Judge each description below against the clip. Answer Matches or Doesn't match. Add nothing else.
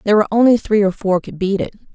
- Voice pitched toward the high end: Matches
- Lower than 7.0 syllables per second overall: Doesn't match